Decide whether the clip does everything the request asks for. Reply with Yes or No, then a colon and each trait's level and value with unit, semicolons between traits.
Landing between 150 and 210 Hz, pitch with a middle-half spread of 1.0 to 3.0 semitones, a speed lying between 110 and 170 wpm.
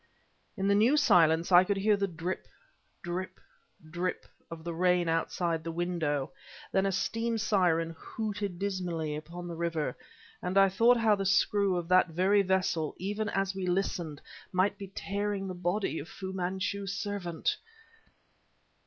Yes: medium, 185 Hz; average, 2.7 semitones; average, 155 wpm